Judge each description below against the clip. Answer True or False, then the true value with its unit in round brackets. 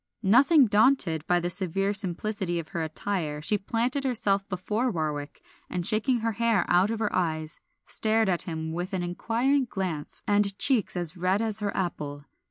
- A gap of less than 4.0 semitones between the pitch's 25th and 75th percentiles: False (4.3 semitones)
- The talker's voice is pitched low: False (195 Hz)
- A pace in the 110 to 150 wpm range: False (175 wpm)